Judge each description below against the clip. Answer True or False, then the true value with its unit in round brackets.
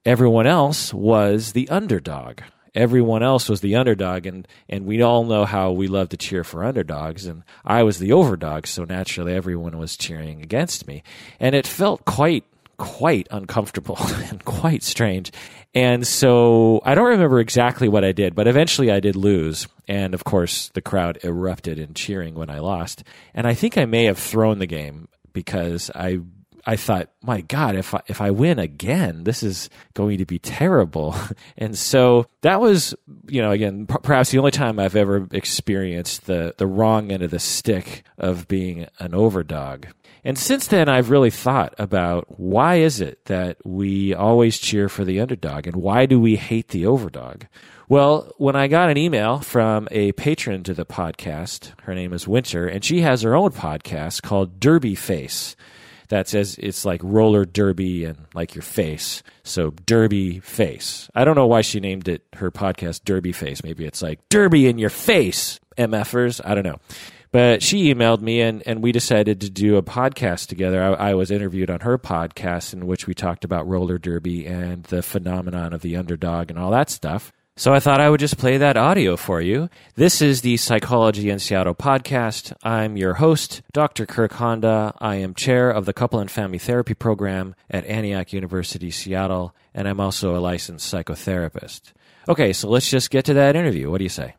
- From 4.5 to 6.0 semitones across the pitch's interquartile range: True (5.0 semitones)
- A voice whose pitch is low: True (105 Hz)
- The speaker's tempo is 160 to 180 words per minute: False (190 wpm)